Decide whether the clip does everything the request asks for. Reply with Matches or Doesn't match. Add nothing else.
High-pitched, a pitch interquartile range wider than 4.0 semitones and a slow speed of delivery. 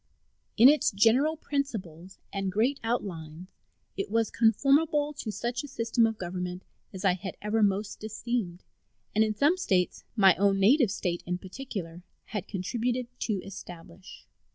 Doesn't match